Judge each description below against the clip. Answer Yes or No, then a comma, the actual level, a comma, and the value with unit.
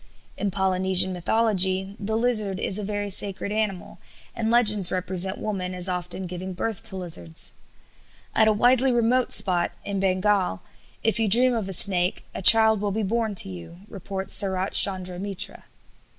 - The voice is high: Yes, high, 195 Hz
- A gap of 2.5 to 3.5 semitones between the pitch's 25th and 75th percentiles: Yes, average, 2.9 semitones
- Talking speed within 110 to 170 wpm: Yes, average, 165 wpm